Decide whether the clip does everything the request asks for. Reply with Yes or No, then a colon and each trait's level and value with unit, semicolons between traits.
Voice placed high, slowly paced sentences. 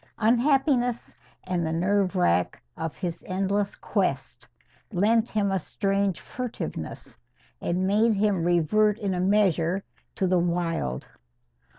Yes: high, 195 Hz; slow, 120 wpm